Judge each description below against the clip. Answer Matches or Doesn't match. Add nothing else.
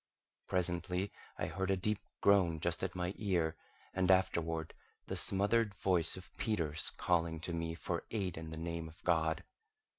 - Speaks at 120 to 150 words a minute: Doesn't match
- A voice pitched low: Matches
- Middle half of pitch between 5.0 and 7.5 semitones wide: Doesn't match